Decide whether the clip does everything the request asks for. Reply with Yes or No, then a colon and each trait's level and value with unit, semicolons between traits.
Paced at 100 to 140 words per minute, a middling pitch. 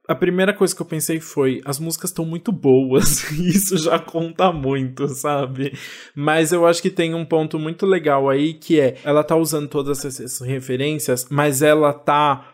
No: fast, 185 wpm; medium, 155 Hz